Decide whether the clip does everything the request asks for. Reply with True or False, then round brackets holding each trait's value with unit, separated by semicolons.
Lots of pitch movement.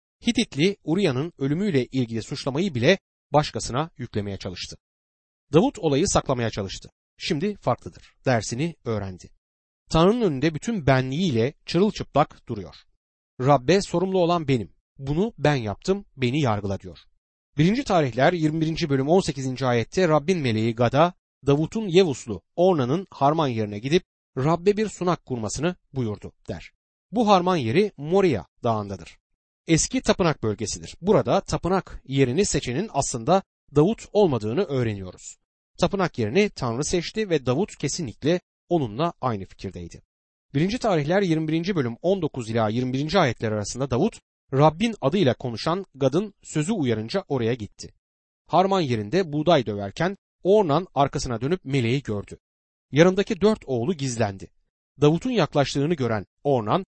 True (7.6 semitones)